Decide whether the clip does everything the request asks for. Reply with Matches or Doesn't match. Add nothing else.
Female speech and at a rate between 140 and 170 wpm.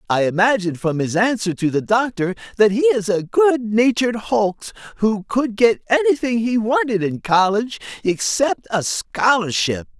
Doesn't match